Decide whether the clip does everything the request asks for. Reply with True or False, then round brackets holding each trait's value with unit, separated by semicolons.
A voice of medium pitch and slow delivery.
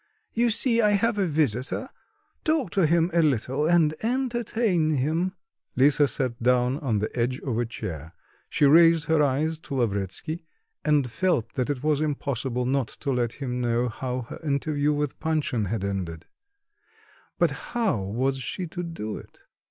False (145 Hz; 165 wpm)